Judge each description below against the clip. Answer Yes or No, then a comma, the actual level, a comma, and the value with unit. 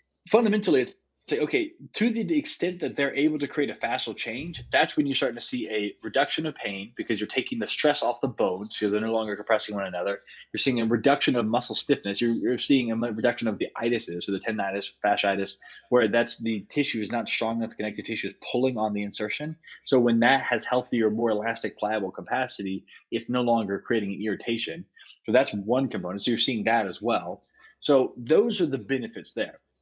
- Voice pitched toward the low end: Yes, low, 115 Hz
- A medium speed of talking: No, fast, 210 wpm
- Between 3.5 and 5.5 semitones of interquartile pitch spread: Yes, average, 4.7 semitones